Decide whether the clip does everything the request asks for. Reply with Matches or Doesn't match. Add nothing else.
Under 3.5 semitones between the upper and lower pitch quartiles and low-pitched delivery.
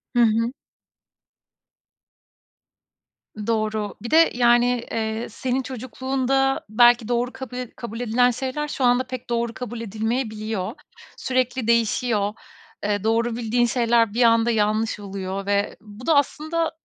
Doesn't match